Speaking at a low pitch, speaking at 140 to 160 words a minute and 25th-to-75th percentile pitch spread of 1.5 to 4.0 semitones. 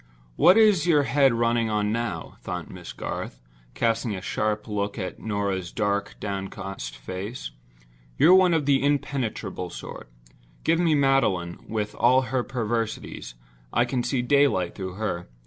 No: low, 115 Hz; average, 145 wpm; average, 5.3 semitones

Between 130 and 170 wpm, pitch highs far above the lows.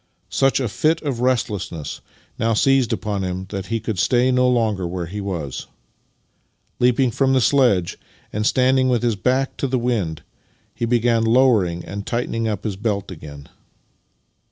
No: average, 160 wpm; average, 4.6 semitones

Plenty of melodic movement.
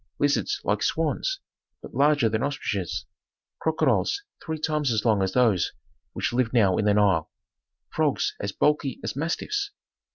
Yes: wide, 6.5 semitones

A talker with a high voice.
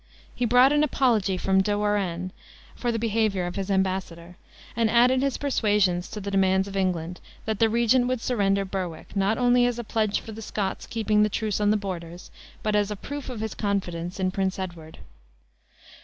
Yes: high, 205 Hz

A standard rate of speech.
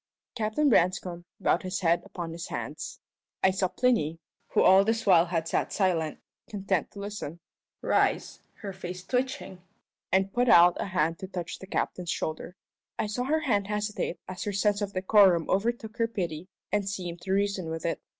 Yes: average, 180 wpm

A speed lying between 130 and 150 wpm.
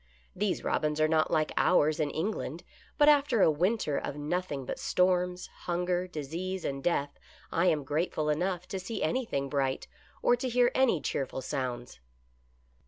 No: average, 170 wpm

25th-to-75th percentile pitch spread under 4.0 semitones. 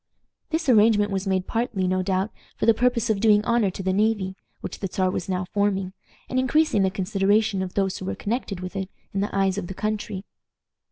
Yes: narrow, 2.6 semitones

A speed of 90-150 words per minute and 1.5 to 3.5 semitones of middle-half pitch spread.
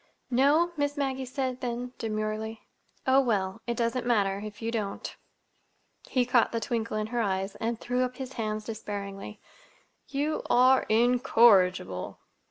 Yes: slow, 135 wpm; average, 3.1 semitones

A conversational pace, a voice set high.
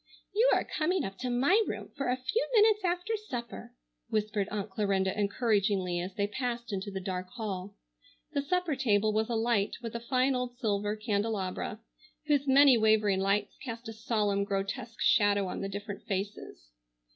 Yes: average, 170 wpm; high, 215 Hz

